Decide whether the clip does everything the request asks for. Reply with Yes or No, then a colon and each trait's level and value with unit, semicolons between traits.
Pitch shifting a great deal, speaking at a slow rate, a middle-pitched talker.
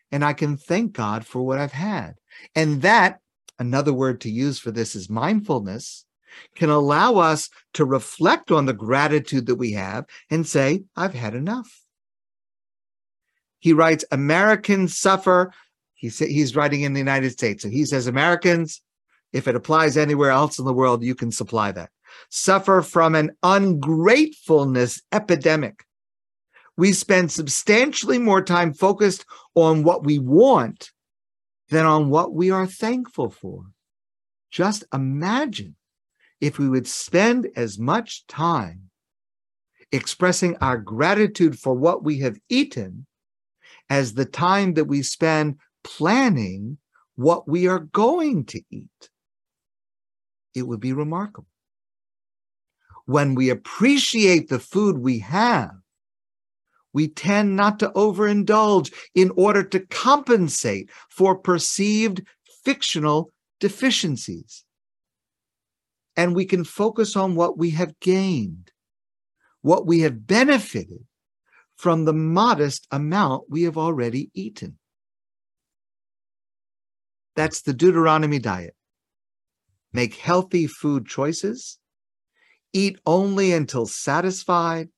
Yes: wide, 6.0 semitones; slow, 120 wpm; medium, 160 Hz